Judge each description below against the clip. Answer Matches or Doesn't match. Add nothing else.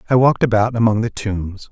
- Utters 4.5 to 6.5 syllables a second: Matches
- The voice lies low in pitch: Matches